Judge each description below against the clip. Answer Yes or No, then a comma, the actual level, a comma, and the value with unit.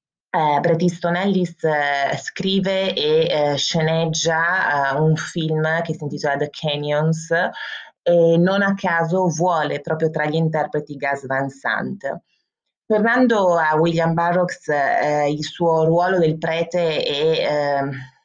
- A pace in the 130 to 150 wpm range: Yes, average, 135 wpm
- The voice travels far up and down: No, average, 3.1 semitones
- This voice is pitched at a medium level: Yes, medium, 160 Hz